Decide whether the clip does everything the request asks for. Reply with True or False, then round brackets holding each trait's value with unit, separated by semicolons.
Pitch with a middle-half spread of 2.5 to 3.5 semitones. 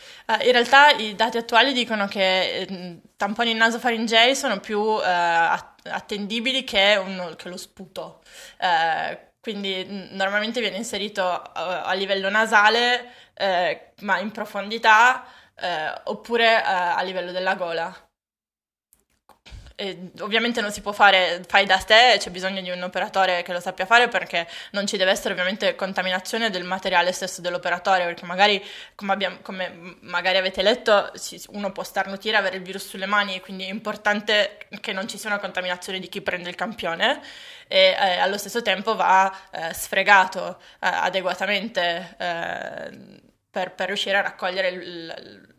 True (2.8 semitones)